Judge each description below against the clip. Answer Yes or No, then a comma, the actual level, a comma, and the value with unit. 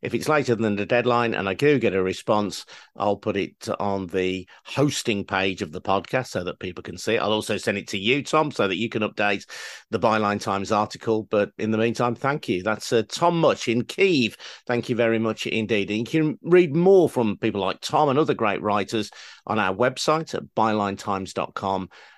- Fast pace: Yes, fast, 215 wpm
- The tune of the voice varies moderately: Yes, average, 3.4 semitones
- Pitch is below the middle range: Yes, low, 110 Hz